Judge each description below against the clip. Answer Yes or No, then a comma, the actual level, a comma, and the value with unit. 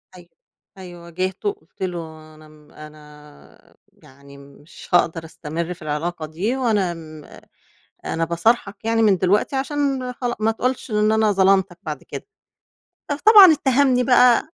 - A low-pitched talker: No, medium, 185 Hz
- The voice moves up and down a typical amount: No, wide, 7.4 semitones